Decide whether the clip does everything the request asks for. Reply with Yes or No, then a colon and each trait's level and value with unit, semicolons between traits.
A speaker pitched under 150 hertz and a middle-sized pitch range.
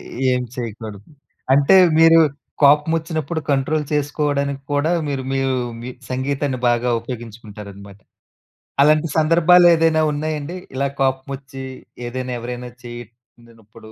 Yes: low, 135 Hz; average, 4.1 semitones